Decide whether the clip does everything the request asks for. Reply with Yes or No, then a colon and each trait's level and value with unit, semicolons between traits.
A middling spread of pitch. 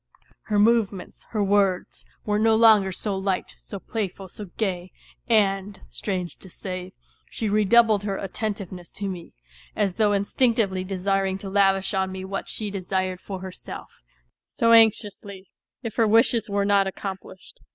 No: narrow, 2.0 semitones